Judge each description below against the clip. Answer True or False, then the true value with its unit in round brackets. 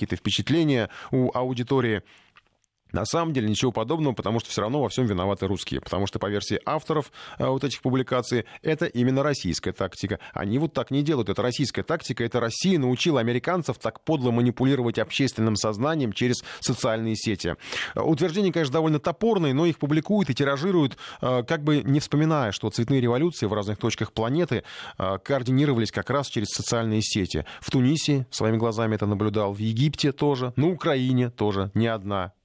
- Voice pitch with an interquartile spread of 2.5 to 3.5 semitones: False (5.2 semitones)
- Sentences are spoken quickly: True (170 wpm)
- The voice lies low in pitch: True (125 Hz)